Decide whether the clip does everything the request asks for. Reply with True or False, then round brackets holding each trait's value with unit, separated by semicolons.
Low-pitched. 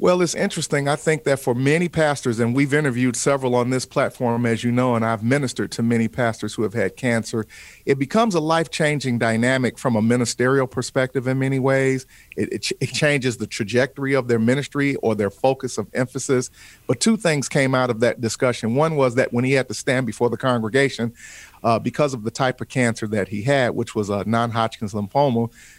True (125 Hz)